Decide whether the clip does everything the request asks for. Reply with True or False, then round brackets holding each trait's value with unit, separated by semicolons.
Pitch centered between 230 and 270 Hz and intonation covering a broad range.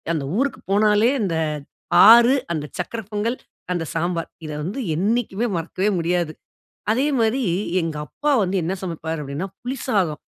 False (190 Hz; 5.8 semitones)